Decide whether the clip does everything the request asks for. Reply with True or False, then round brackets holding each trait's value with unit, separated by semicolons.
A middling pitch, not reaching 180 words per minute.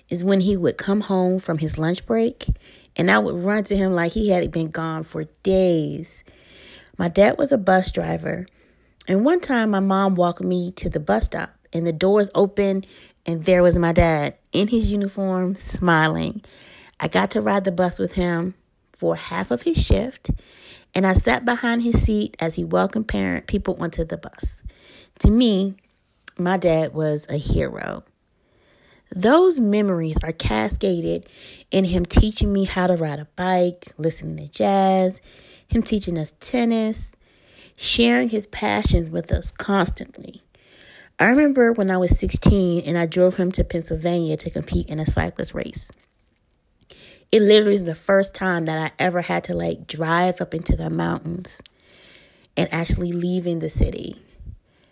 True (180 Hz; 165 wpm)